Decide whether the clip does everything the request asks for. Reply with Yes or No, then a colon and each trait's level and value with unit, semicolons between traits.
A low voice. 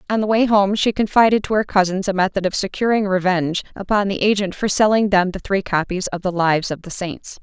No: high, 195 Hz